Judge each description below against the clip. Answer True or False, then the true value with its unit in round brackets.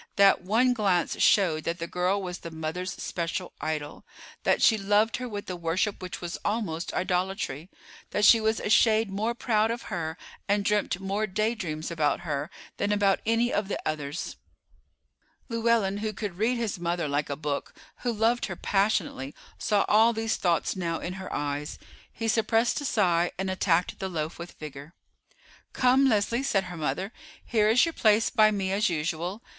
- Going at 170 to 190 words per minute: True (180 wpm)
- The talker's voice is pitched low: False (195 Hz)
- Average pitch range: True (4.3 semitones)